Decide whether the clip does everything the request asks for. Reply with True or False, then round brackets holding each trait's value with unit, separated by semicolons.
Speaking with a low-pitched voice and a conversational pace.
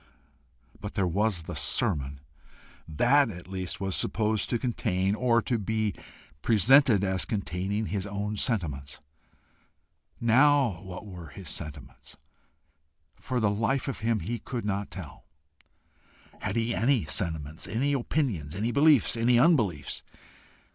False (105 Hz; 130 wpm)